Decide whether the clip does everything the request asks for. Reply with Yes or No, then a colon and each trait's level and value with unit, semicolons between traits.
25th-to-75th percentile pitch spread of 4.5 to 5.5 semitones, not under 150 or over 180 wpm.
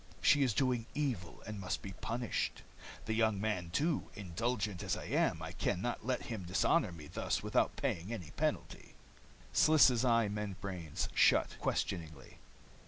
Yes: average, 5.0 semitones; average, 155 wpm